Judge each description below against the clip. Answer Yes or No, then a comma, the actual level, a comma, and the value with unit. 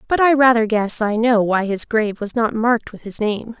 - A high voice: Yes, high, 225 Hz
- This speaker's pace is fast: Yes, fast, 250 wpm